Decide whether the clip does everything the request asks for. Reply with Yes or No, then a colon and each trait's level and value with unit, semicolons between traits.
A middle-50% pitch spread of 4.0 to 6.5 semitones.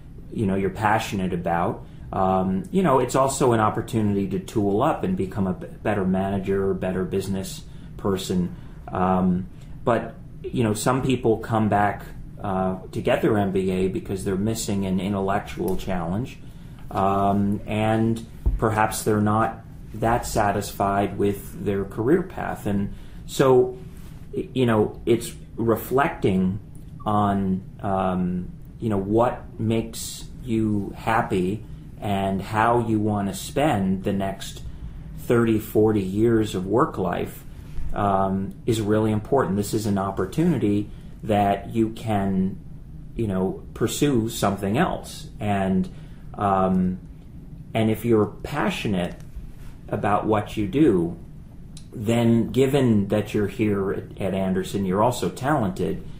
No: average, 3.1 semitones